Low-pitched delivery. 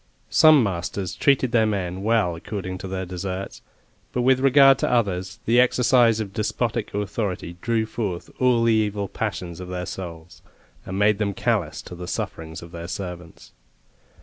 Yes: low, 100 Hz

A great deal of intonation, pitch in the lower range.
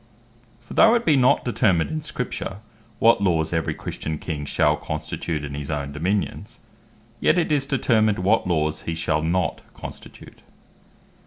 Yes: wide, 7.4 semitones; very low, 90 Hz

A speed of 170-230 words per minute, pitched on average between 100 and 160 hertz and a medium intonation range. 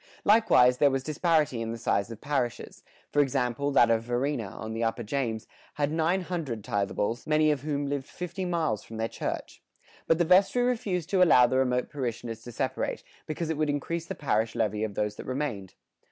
No: average, 195 wpm; medium, 140 Hz; wide, 5.8 semitones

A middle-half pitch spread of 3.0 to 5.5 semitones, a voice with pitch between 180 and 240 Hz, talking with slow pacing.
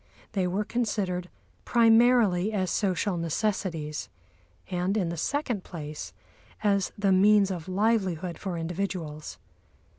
Yes: average, 3.4 semitones; high, 190 Hz; slow, 115 wpm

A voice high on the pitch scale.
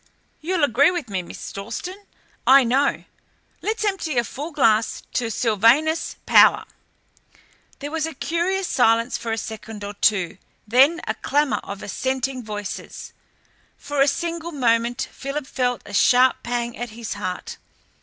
Yes: very high, 255 Hz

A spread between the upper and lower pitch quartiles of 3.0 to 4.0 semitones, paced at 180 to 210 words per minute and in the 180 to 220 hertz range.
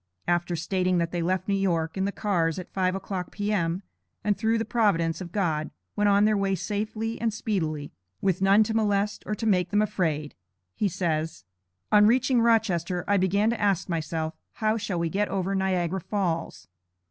Yes: average, 3.4 semitones; average, 185 wpm; high, 190 Hz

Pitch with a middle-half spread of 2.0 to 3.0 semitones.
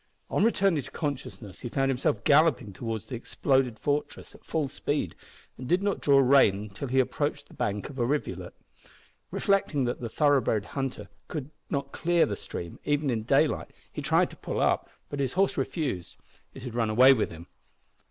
No: average, 4.1 semitones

